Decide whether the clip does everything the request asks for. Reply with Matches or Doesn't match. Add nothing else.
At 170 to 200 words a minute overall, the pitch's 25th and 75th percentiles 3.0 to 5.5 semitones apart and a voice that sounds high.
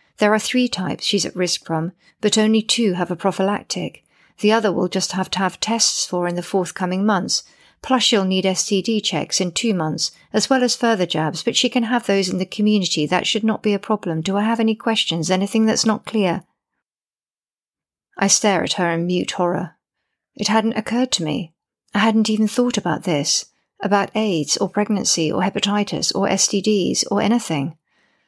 Matches